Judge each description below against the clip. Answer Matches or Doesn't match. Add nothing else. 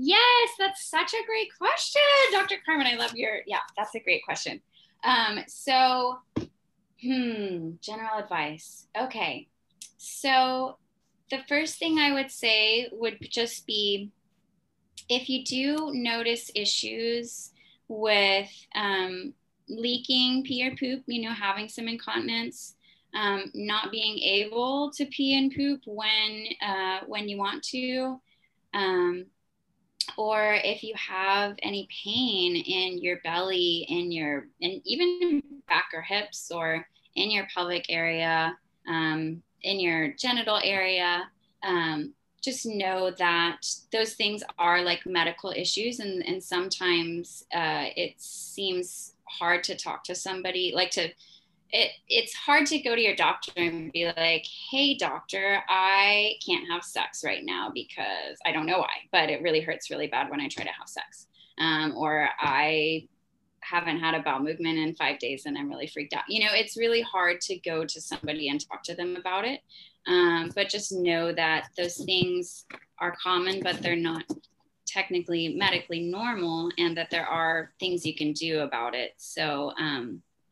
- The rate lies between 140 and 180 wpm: Matches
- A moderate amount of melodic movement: Doesn't match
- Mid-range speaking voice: Doesn't match